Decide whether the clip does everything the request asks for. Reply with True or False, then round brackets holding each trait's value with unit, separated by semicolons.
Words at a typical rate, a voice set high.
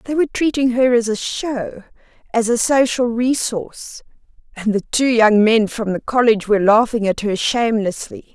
True (170 wpm; 225 Hz)